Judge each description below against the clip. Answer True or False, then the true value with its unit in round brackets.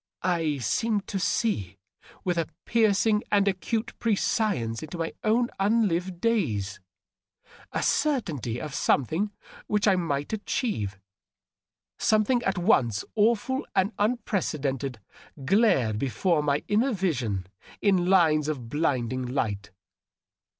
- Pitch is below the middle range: False (180 Hz)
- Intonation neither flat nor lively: False (8.1 semitones)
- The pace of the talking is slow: True (125 wpm)